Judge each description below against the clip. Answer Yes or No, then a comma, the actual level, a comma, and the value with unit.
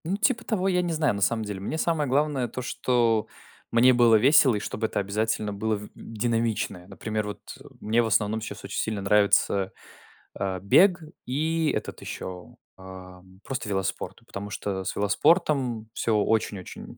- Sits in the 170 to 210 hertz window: No, low, 110 Hz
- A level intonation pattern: No, average, 4.9 semitones